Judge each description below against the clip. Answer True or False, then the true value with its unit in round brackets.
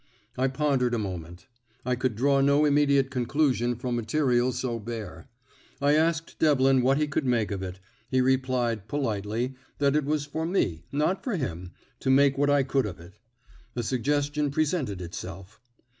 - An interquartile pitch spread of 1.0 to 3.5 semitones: False (4.0 semitones)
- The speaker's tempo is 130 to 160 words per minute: False (170 wpm)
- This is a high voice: False (130 Hz)